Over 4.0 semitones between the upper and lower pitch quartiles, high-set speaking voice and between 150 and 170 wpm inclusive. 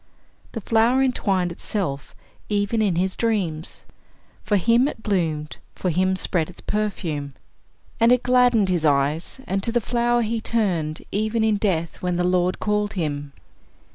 Yes: average, 4.9 semitones; high, 195 Hz; average, 155 wpm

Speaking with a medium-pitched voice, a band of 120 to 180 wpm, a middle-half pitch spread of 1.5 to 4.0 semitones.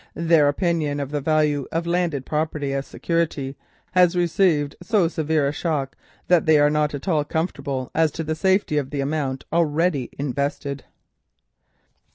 Yes: medium, 150 Hz; average, 160 wpm; average, 2.9 semitones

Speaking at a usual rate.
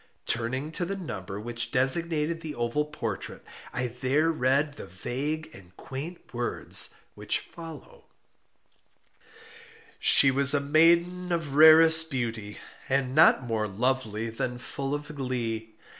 No: slow, 130 wpm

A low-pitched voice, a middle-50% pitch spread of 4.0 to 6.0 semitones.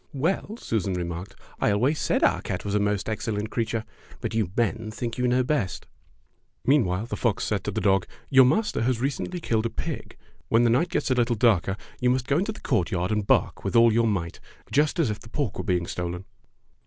Yes: low, 115 Hz; average, 4.3 semitones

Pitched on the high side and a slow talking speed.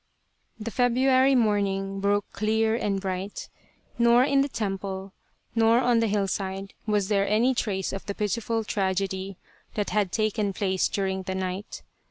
No: high, 205 Hz; average, 150 wpm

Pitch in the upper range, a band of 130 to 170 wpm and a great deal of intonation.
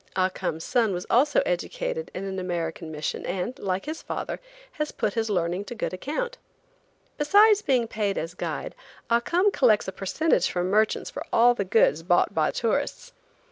No: high, 215 Hz; average, 180 wpm; wide, 8.1 semitones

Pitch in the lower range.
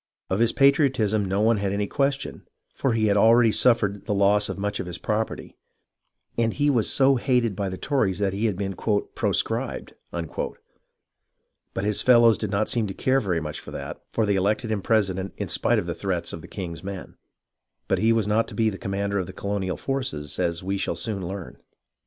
Yes: low, 105 Hz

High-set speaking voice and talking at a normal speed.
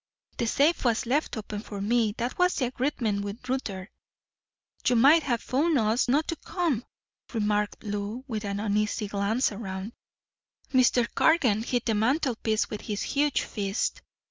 Yes: high, 230 Hz; average, 155 wpm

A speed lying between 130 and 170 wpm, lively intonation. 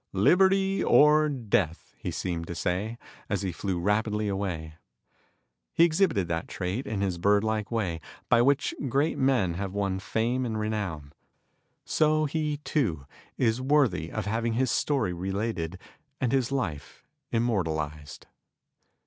Yes: average, 140 wpm; wide, 6.5 semitones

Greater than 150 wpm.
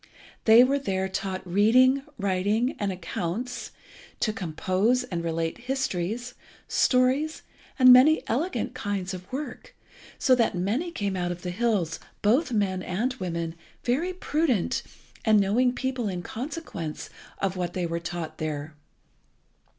No: slow, 135 wpm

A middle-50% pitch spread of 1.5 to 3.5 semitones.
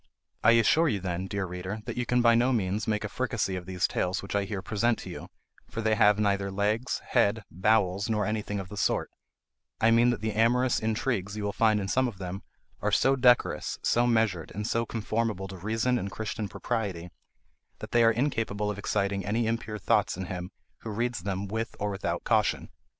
Yes: average, 2.8 semitones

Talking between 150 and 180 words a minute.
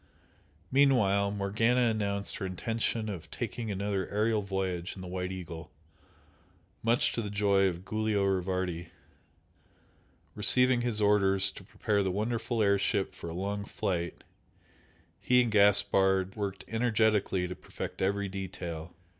No: slow, 135 wpm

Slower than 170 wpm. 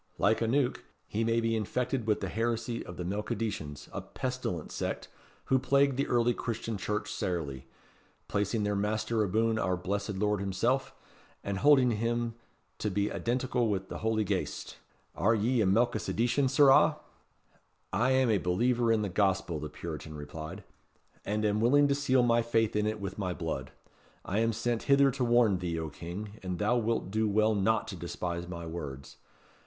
No: average, 175 wpm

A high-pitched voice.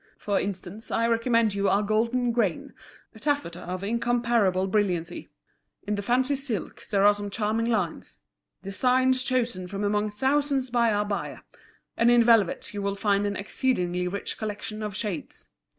Yes: high, 210 Hz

